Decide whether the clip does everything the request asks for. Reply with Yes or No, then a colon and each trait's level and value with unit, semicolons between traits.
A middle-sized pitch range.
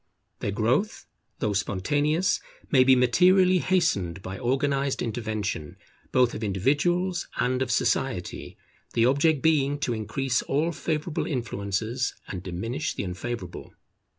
No: wide, 6.0 semitones